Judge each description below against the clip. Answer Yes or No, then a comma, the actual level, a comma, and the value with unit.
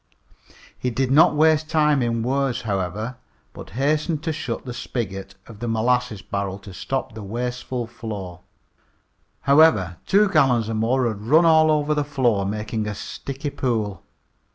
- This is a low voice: Yes, low, 120 Hz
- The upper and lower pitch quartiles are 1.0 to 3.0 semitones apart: No, average, 5.3 semitones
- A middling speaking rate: Yes, average, 155 wpm